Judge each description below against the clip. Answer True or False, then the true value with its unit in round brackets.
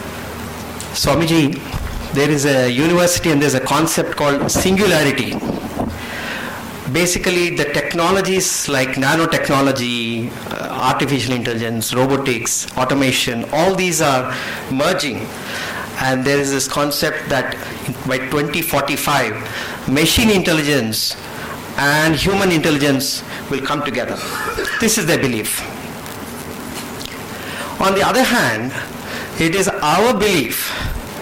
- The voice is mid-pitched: True (145 Hz)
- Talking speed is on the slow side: True (105 wpm)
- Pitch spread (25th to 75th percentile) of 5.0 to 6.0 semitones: False (4.3 semitones)